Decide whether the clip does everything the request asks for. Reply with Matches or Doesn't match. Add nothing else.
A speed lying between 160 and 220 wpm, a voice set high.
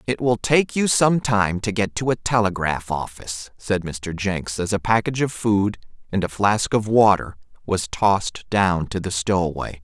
Doesn't match